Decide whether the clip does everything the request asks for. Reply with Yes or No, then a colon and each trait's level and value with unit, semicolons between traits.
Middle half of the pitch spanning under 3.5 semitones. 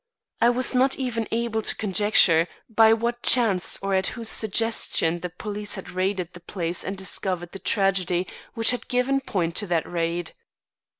No: average, 4.3 semitones